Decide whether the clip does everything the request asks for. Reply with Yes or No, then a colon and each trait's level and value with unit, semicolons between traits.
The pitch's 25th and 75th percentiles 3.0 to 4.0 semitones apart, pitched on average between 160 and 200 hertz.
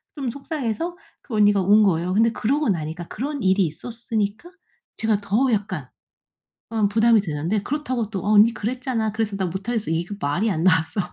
No: average, 3.7 semitones; high, 215 Hz